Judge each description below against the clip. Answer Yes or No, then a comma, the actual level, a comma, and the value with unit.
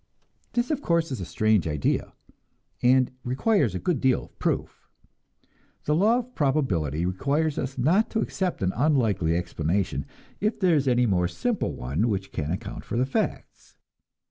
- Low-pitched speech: Yes, low, 125 Hz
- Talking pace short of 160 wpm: No, average, 165 wpm